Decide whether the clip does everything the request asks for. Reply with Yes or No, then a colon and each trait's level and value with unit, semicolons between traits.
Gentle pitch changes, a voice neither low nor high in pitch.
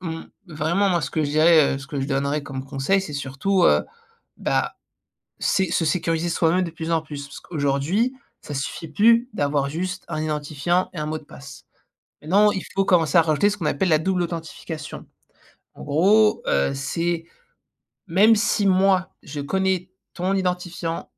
No: average, 4.1 semitones; medium, 165 Hz